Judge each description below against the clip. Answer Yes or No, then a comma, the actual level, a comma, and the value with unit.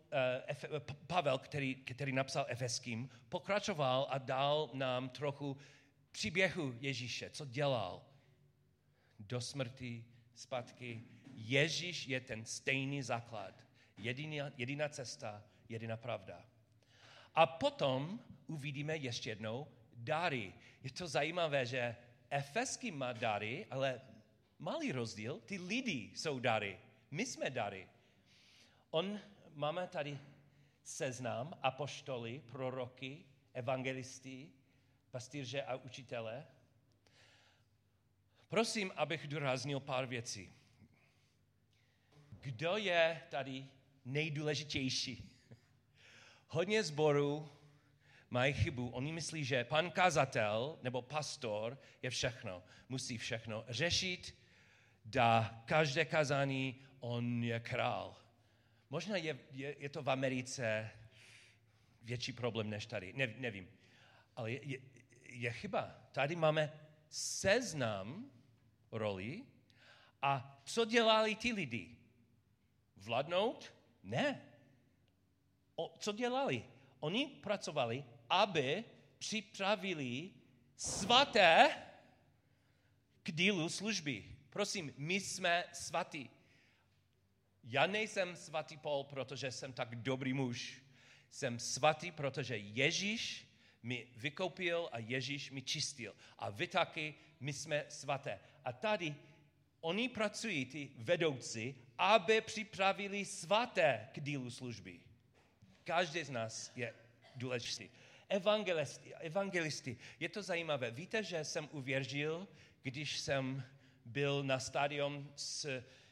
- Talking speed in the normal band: No, slow, 100 wpm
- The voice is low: Yes, low, 130 Hz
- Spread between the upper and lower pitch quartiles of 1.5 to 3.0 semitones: No, average, 4.2 semitones